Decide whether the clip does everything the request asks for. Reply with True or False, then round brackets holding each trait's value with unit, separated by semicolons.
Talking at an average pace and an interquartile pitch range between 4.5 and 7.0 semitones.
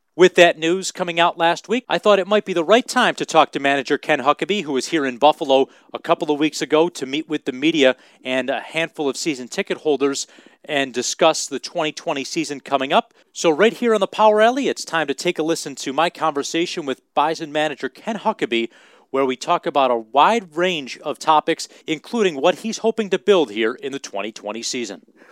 False (215 wpm; 4.9 semitones)